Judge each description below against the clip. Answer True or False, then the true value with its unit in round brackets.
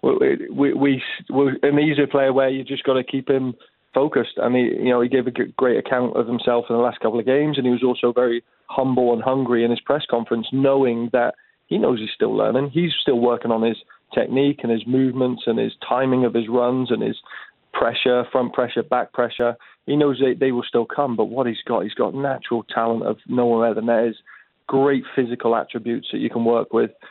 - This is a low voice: True (125 Hz)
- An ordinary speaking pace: False (225 wpm)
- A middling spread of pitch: False (2.2 semitones)